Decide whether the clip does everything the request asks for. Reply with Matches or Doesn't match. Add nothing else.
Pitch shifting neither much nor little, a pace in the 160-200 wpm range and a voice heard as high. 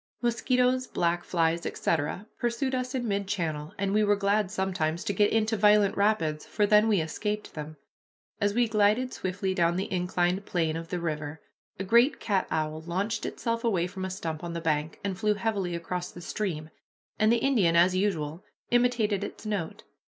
Matches